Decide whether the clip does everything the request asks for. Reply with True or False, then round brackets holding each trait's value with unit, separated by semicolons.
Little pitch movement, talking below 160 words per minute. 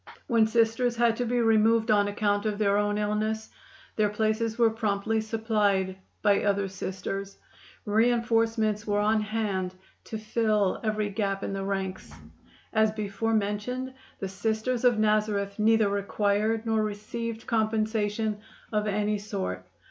True (1.7 semitones; 140 wpm)